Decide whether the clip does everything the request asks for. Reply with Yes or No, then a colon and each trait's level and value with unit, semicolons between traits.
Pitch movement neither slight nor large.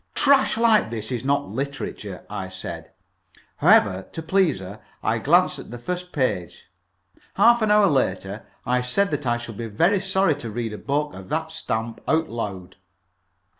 No: wide, 8.3 semitones